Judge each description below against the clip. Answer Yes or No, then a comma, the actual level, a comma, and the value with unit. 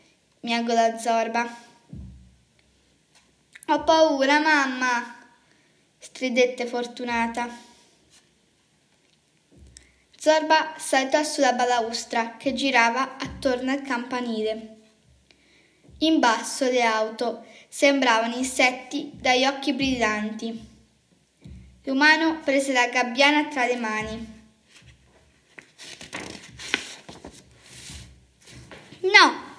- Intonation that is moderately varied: Yes, average, 3.3 semitones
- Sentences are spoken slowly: Yes, slow, 65 wpm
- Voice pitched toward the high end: Yes, high, 240 Hz